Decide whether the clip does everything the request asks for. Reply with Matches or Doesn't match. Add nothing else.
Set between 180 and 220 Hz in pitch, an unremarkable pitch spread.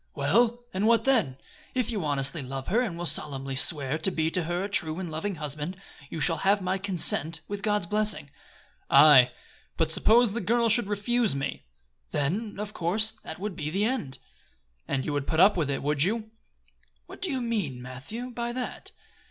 Doesn't match